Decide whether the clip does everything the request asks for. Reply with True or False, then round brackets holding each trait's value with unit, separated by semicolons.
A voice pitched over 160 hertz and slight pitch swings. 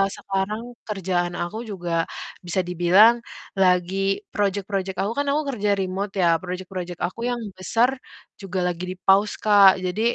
True (190 Hz; 2.3 semitones)